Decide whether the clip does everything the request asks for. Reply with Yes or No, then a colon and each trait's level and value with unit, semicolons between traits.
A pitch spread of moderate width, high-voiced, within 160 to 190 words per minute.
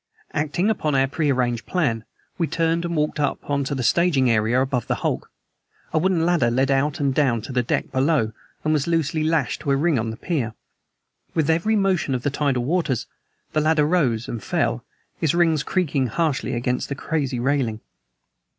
No: average, 4.2 semitones; medium, 145 Hz; average, 185 wpm